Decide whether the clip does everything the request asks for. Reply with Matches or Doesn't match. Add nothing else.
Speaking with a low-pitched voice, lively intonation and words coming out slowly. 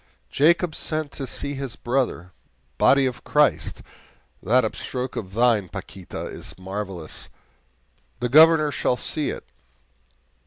Matches